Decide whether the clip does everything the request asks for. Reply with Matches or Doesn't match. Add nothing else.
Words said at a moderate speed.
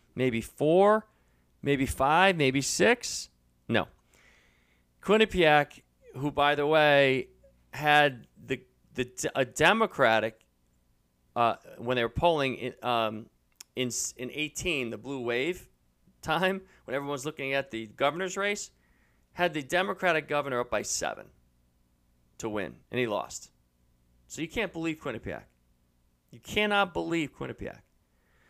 Doesn't match